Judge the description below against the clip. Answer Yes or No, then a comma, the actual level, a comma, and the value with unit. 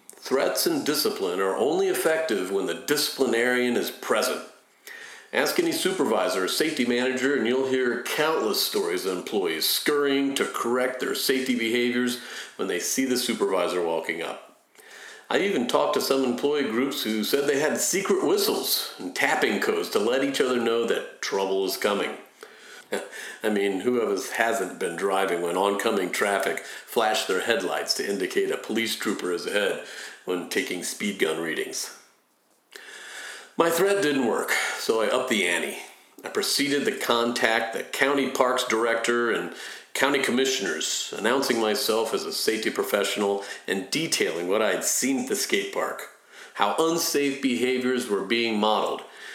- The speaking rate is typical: Yes, average, 155 wpm